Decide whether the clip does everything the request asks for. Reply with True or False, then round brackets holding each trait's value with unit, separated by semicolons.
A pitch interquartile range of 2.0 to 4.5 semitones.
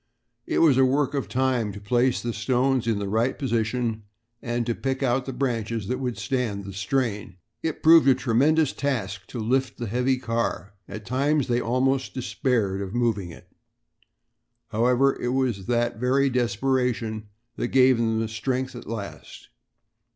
True (2.9 semitones)